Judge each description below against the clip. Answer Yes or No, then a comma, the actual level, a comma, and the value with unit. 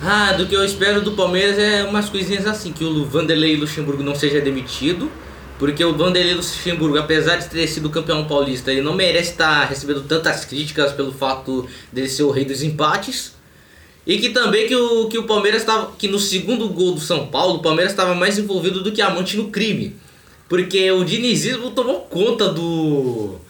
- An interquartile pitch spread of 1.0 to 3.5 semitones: No, wide, 5.4 semitones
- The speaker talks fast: Yes, fast, 195 wpm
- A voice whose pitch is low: No, medium, 175 Hz